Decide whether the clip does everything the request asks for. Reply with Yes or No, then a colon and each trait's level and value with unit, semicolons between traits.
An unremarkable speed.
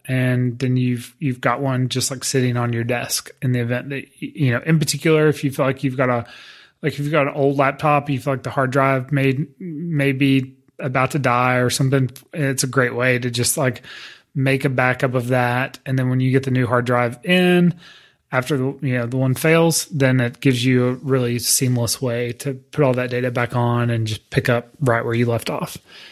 No: fast, 230 wpm